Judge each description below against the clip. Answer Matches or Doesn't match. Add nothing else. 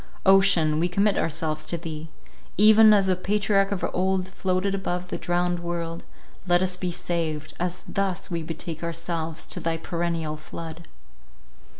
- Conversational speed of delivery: Matches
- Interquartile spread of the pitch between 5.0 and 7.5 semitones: Doesn't match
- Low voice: Doesn't match